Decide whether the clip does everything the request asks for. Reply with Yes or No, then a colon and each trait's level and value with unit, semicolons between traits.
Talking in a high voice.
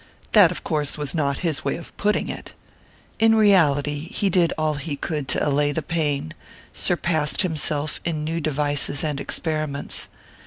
No: medium, 155 Hz